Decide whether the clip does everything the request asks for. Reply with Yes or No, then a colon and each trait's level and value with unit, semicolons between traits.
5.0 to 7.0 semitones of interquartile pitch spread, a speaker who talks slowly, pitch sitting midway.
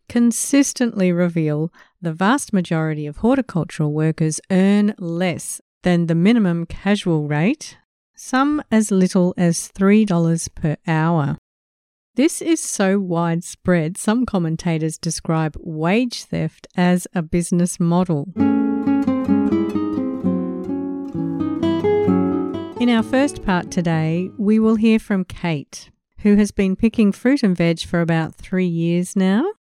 Yes: average, 5.3 semitones; slow, 115 wpm; medium, 180 Hz